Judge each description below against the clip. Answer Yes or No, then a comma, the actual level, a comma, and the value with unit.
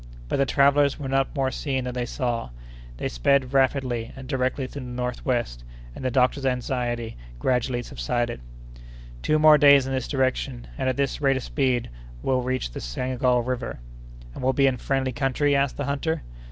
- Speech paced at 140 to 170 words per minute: No, average, 190 wpm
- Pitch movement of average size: No, narrow, 1.9 semitones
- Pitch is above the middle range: No, low, 130 Hz